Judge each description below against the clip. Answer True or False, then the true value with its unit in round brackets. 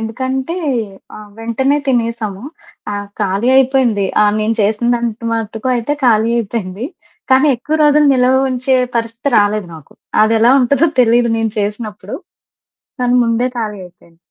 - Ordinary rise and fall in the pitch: True (3.1 semitones)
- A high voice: True (230 Hz)